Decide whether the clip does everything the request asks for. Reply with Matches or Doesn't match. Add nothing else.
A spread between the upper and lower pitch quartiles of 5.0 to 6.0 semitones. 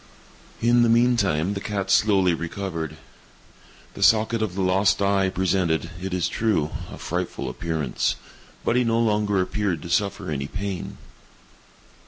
Doesn't match